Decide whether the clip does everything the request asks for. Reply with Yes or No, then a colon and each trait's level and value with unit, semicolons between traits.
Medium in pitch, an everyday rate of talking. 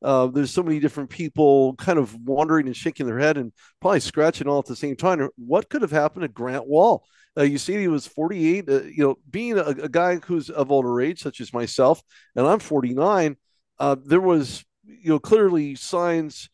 No: medium, 150 Hz; fast, 210 wpm